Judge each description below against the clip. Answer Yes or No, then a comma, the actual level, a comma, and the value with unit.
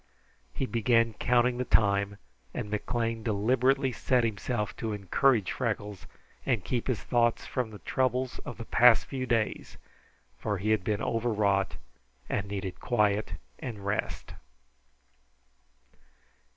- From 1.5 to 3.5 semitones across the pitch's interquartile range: Yes, average, 3.2 semitones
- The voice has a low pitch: Yes, low, 115 Hz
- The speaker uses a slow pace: Yes, slow, 125 wpm